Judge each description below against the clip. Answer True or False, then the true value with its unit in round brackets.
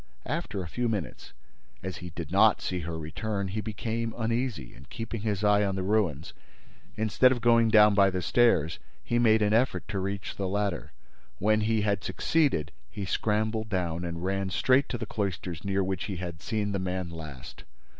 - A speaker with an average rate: True (190 wpm)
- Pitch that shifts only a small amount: False (3.3 semitones)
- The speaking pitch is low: True (100 Hz)